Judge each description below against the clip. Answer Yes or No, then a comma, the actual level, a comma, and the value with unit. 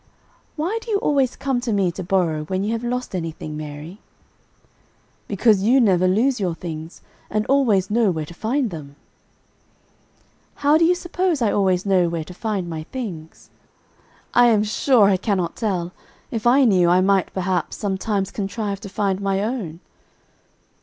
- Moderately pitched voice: No, high, 200 Hz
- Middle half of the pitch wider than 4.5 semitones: Yes, average, 5.0 semitones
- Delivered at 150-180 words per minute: Yes, average, 165 wpm